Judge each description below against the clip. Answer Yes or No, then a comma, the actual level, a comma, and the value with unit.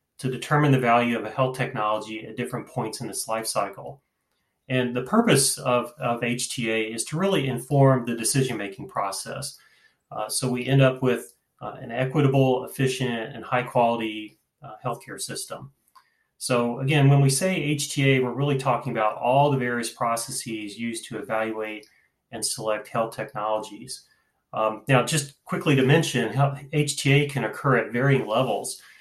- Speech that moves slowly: No, average, 160 wpm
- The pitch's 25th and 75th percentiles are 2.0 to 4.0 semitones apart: Yes, average, 3.5 semitones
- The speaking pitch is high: No, low, 125 Hz